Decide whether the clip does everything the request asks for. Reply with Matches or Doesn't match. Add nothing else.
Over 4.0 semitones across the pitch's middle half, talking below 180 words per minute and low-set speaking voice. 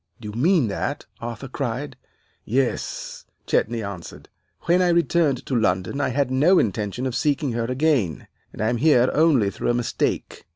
Matches